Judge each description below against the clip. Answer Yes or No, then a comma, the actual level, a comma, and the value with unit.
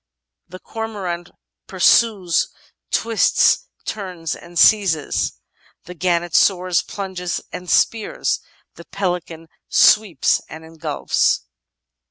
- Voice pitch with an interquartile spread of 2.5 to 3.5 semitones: Yes, average, 2.8 semitones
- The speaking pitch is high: No, medium, 180 Hz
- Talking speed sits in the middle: No, slow, 90 wpm